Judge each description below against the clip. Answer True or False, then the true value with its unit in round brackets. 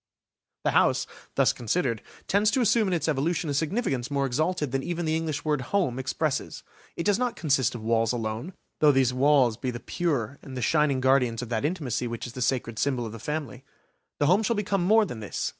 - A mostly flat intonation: False (5.6 semitones)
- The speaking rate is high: True (210 wpm)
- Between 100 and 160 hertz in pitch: True (140 Hz)